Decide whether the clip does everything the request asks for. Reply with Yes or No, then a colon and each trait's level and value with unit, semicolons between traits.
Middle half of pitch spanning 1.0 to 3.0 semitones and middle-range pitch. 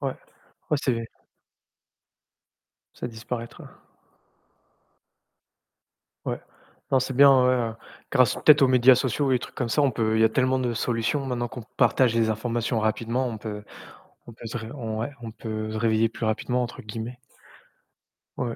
No: narrow, 2.4 semitones; low, 120 Hz